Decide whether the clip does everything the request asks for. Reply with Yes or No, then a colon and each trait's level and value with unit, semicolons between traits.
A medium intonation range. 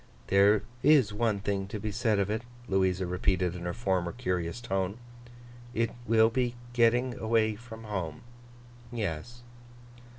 Yes: average, 3.6 semitones